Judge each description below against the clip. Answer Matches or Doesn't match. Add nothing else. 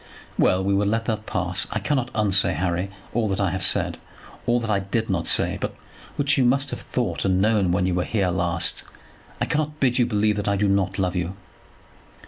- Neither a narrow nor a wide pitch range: Matches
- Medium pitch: Doesn't match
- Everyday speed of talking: Doesn't match